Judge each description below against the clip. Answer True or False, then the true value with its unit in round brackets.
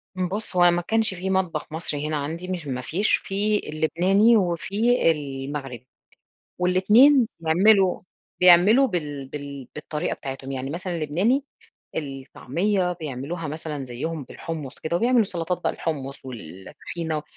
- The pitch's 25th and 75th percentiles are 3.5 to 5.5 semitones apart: True (4.8 semitones)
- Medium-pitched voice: True (165 Hz)